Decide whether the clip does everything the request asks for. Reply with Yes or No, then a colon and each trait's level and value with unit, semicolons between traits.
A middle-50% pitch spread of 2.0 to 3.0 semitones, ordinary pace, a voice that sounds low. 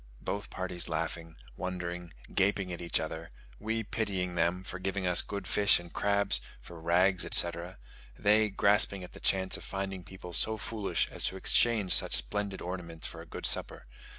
Yes: narrow, 2.6 semitones; average, 175 wpm; very low, 95 Hz